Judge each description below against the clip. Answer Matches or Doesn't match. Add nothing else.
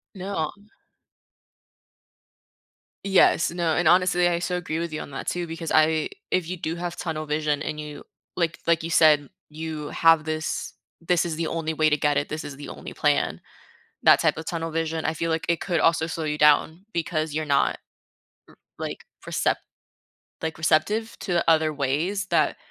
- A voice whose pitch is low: Doesn't match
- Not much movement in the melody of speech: Matches